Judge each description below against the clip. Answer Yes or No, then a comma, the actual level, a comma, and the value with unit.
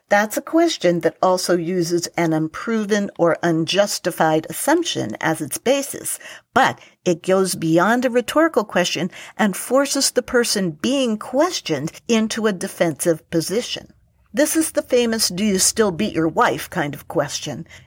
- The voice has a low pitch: No, high, 200 Hz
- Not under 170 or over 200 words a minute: No, average, 150 wpm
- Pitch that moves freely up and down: Yes, wide, 6.3 semitones